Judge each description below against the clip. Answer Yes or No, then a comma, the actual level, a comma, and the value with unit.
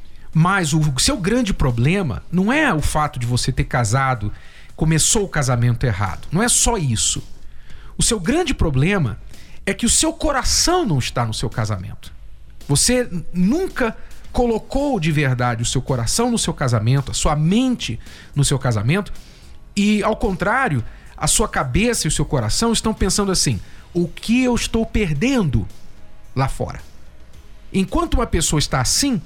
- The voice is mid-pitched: Yes, medium, 155 Hz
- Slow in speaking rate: No, average, 160 wpm